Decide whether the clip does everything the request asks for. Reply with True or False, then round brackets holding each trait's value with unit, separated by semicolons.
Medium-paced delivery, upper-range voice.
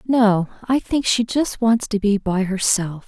True (195 wpm; 215 Hz)